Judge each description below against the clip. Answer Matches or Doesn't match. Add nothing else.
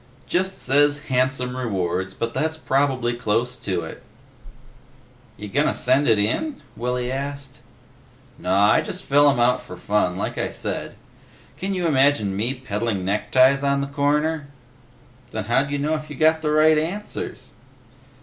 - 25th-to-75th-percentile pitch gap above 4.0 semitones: Matches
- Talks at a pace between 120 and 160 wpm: Matches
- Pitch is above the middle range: Doesn't match